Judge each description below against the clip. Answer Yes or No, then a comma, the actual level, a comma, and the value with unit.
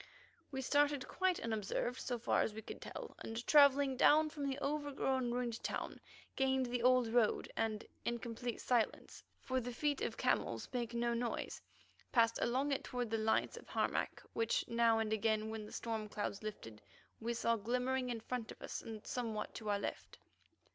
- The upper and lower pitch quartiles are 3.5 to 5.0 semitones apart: No, average, 2.7 semitones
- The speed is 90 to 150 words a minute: No, average, 180 wpm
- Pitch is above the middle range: Yes, high, 235 Hz